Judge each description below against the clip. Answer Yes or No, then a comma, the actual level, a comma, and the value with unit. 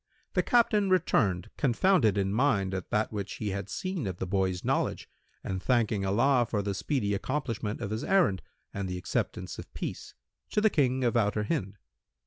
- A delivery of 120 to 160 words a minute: No, average, 180 wpm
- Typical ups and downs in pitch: No, wide, 5.7 semitones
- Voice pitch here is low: Yes, low, 105 Hz